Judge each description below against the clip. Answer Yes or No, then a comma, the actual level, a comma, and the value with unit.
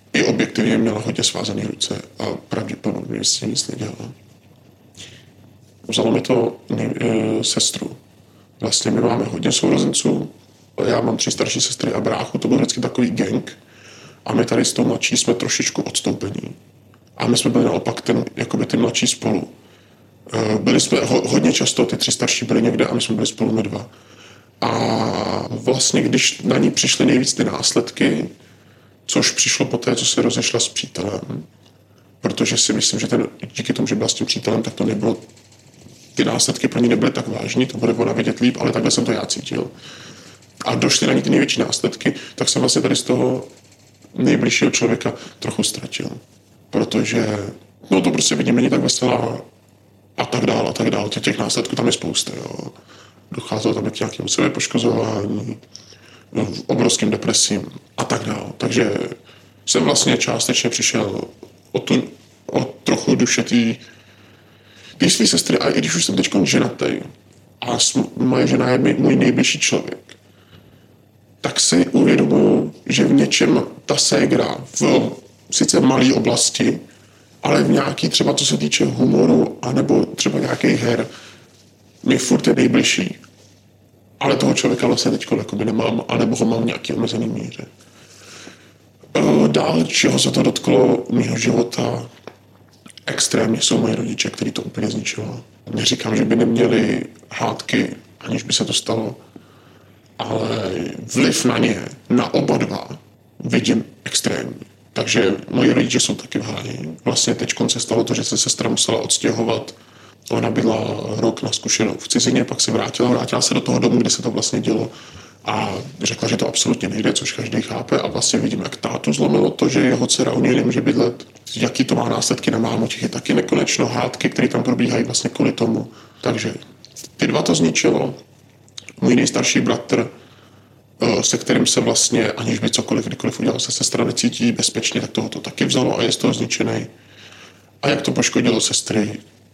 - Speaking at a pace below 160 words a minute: No, average, 165 wpm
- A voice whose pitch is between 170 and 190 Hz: No, low, 115 Hz